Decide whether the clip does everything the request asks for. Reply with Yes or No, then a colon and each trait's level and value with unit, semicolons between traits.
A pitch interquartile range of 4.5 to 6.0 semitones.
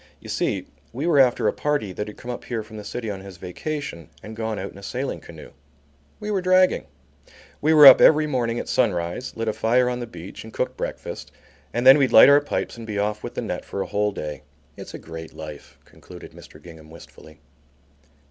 Yes: wide, 5.4 semitones